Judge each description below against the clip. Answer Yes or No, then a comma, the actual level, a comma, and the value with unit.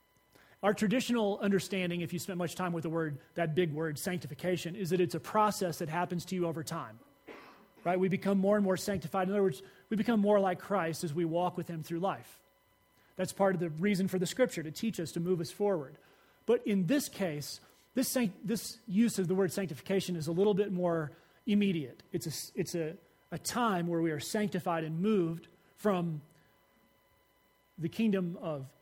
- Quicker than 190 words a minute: Yes, average, 200 wpm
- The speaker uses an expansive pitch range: No, average, 3.2 semitones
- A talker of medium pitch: Yes, medium, 180 Hz